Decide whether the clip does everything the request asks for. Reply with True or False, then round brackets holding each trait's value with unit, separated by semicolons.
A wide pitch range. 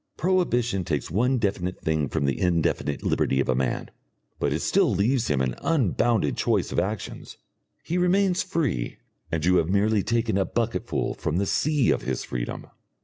True (7.8 semitones)